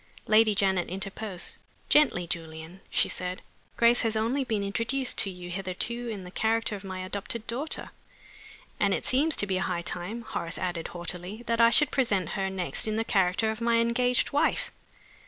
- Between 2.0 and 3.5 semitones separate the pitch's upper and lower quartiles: No, average, 4.2 semitones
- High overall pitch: Yes, high, 205 Hz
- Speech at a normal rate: Yes, average, 180 wpm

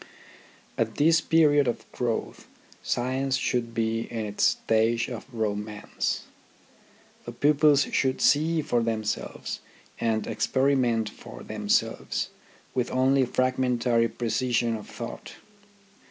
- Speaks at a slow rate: Yes, slow, 110 wpm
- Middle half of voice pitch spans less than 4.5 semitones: Yes, average, 2.9 semitones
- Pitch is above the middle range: No, low, 120 Hz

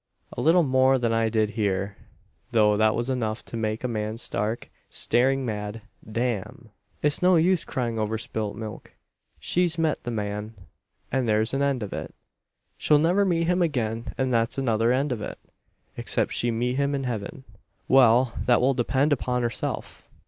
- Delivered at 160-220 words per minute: Yes, average, 175 wpm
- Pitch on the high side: No, low, 120 Hz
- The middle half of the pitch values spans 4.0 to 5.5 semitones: No, average, 3.6 semitones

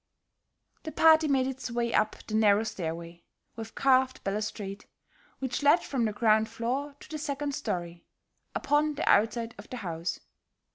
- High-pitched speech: Yes, high, 230 Hz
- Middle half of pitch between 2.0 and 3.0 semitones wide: No, average, 5.0 semitones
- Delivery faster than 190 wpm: No, average, 155 wpm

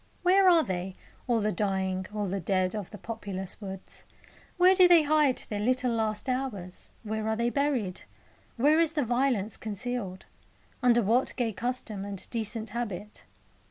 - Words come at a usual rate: Yes, average, 160 wpm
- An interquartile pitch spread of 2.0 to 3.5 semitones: No, average, 4.4 semitones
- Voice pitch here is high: Yes, high, 220 Hz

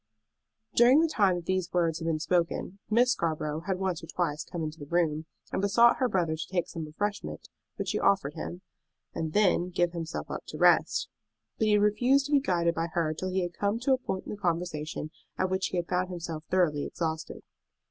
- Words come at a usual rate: No, fast, 220 wpm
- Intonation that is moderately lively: Yes, average, 3.6 semitones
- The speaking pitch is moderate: Yes, medium, 175 Hz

